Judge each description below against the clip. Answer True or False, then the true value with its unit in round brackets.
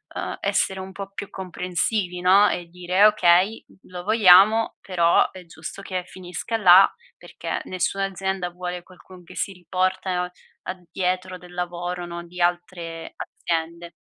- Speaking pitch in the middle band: True (180 Hz)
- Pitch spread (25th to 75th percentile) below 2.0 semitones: True (1.4 semitones)